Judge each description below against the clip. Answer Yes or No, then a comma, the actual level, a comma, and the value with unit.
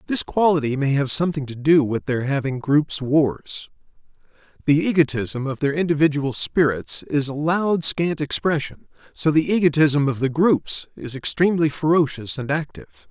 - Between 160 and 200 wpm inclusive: No, average, 150 wpm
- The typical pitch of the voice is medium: Yes, medium, 145 Hz